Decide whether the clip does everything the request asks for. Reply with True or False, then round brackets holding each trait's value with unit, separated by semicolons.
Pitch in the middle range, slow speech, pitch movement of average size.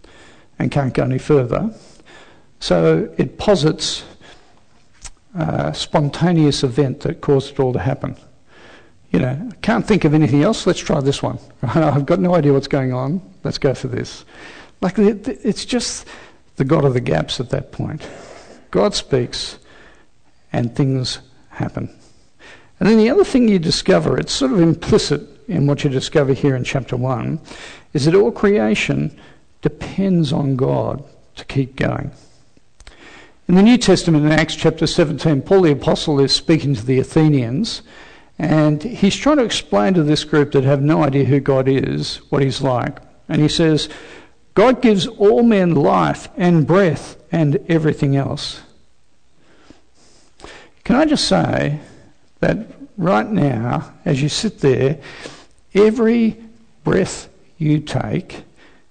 False (150 Hz; 150 wpm; 5.0 semitones)